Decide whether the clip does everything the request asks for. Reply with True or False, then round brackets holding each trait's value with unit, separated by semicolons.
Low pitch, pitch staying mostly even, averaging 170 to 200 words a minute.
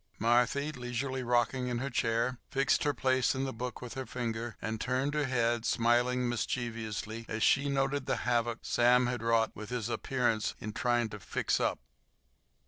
True (120 Hz; 2.1 semitones; 175 wpm)